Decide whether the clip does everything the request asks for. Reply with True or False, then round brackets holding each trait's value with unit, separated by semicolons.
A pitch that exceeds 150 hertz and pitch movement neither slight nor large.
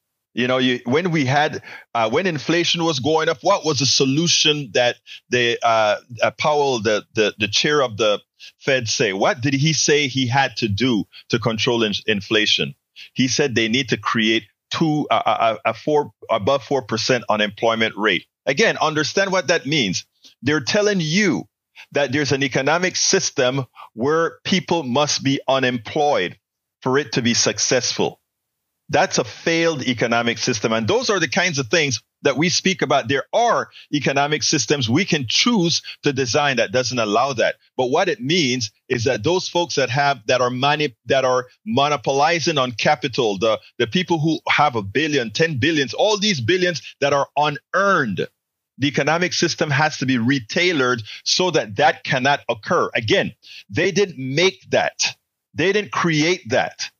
False (140 Hz; 4.6 semitones)